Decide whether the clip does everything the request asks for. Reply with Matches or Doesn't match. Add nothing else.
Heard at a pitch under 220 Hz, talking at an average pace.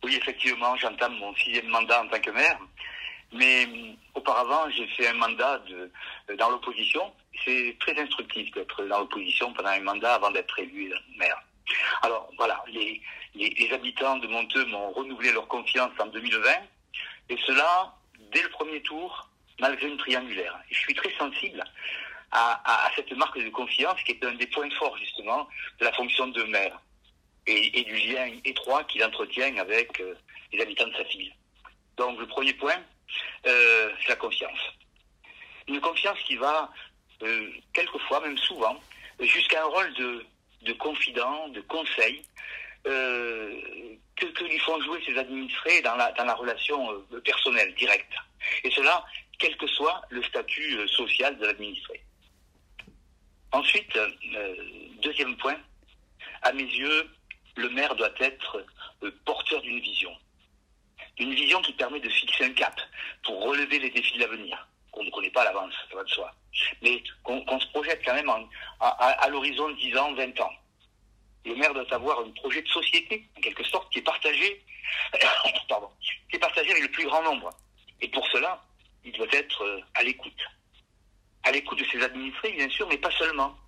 Matches